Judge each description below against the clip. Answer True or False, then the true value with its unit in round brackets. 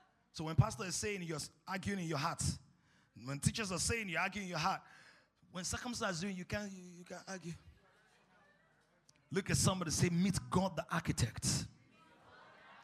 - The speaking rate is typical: True (165 wpm)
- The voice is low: False (175 Hz)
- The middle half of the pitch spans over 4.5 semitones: False (3.4 semitones)